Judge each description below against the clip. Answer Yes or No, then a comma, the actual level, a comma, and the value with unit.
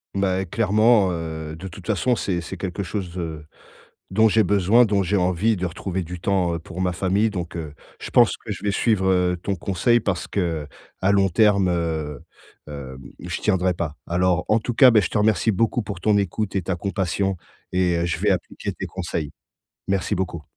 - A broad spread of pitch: No, average, 3.0 semitones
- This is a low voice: Yes, very low, 95 Hz